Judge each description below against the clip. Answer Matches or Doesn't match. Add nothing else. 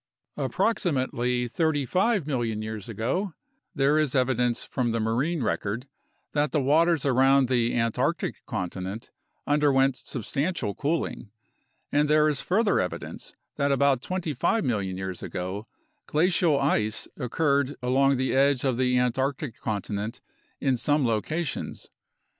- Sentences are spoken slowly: Matches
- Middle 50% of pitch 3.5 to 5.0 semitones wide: Matches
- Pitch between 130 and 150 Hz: Matches